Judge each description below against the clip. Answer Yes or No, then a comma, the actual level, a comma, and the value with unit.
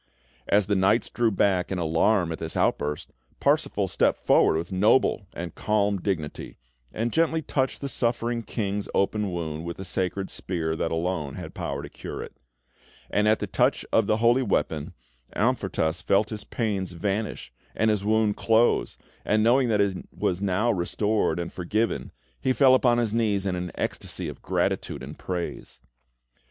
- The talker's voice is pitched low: Yes, low, 100 Hz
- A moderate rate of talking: Yes, average, 170 wpm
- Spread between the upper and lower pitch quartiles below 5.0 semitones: Yes, average, 3.9 semitones